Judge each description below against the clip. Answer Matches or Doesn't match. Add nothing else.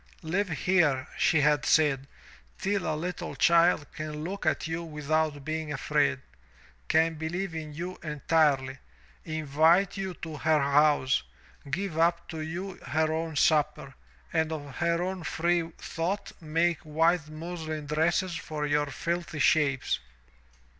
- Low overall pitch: Doesn't match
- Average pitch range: Doesn't match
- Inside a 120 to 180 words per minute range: Matches